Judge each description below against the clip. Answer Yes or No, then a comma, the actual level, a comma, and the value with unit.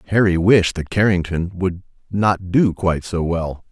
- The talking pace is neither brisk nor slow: Yes, average, 160 wpm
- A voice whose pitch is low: Yes, very low, 90 Hz